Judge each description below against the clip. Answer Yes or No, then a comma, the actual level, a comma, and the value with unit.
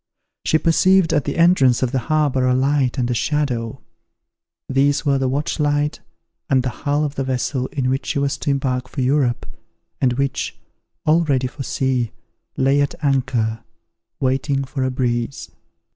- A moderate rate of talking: Yes, average, 165 wpm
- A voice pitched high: No, low, 135 Hz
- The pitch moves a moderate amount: No, narrow, 2.3 semitones